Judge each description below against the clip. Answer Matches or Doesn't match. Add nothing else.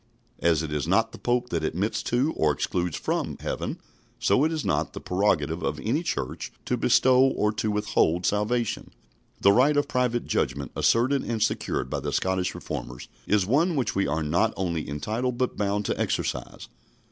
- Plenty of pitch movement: Matches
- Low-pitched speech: Matches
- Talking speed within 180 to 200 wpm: Matches